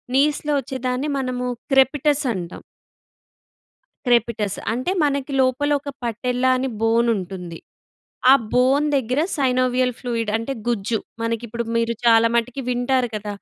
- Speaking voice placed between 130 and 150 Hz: No, very high, 250 Hz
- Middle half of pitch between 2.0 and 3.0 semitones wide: Yes, narrow, 2.6 semitones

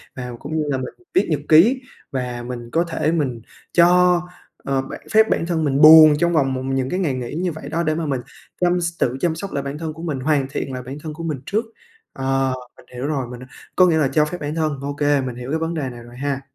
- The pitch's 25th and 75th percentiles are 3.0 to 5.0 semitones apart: Yes, average, 3.8 semitones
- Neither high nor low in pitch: Yes, medium, 150 Hz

